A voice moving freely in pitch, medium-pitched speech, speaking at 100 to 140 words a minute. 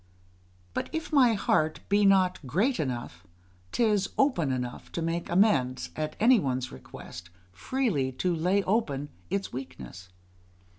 Yes: wide, 8.1 semitones; medium, 170 Hz; slow, 135 wpm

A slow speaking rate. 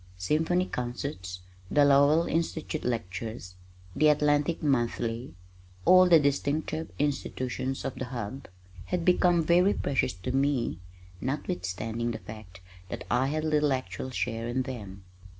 Yes: slow, 130 wpm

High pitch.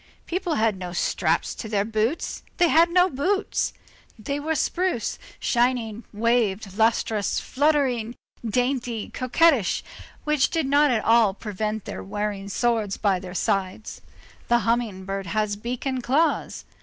Yes: high, 230 Hz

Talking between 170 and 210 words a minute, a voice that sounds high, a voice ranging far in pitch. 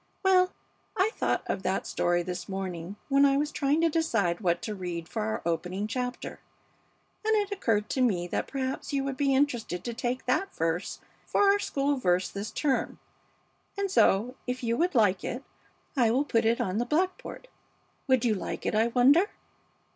Yes: average, 185 wpm; high, 245 Hz; wide, 6.9 semitones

